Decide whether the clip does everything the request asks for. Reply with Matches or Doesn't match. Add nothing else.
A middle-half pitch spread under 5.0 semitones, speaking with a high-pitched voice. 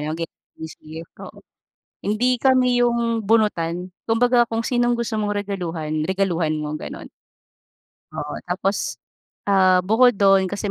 Doesn't match